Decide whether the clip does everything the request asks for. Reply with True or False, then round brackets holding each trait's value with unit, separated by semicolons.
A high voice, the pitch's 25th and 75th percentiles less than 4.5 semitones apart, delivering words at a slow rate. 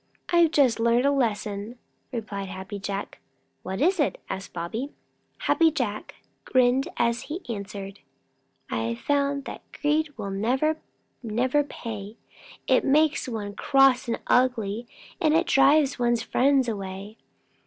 False (240 Hz; 5.5 semitones; 130 wpm)